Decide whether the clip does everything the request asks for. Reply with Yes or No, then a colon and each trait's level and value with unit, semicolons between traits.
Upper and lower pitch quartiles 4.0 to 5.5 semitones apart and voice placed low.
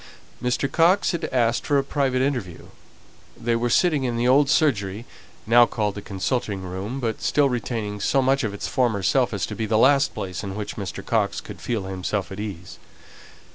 Yes: average, 4.7 semitones; low, 115 Hz